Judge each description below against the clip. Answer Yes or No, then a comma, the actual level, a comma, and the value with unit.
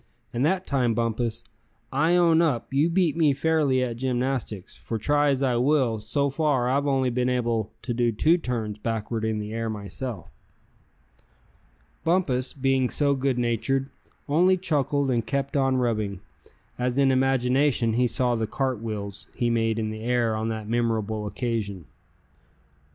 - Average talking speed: Yes, average, 155 wpm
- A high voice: No, low, 125 Hz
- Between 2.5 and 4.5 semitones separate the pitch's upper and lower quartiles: Yes, average, 3.5 semitones